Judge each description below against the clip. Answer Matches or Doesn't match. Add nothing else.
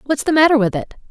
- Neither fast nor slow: Doesn't match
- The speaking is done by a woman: Matches